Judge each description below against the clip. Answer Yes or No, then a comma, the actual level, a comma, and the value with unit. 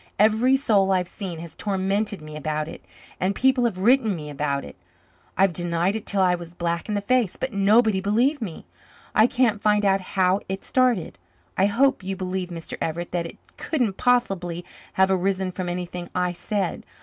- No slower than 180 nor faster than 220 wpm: Yes, average, 185 wpm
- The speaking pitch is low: No, high, 190 Hz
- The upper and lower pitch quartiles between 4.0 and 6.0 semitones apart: No, average, 3.6 semitones